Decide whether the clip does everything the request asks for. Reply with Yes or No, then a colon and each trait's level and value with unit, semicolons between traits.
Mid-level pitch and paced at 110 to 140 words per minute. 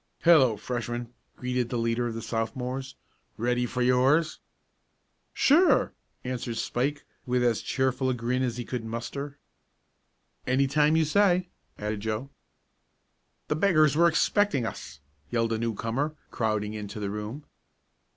No: low, 125 Hz; slow, 135 wpm